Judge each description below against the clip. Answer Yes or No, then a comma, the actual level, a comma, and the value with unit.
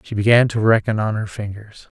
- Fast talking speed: Yes, fast, 210 wpm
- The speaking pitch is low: Yes, low, 105 Hz